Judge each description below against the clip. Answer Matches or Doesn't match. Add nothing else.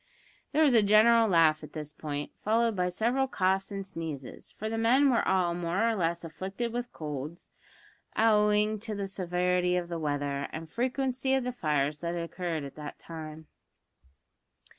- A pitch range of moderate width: Doesn't match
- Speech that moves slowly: Doesn't match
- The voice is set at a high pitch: Doesn't match